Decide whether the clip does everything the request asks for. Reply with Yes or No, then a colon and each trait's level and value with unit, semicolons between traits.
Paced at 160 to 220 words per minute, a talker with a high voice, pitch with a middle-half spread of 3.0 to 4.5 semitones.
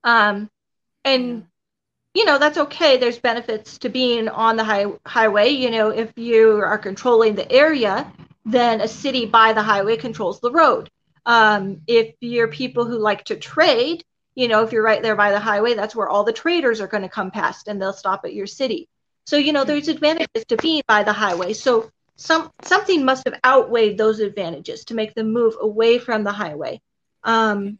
Yes: average, 195 wpm; high, 230 Hz; average, 3.6 semitones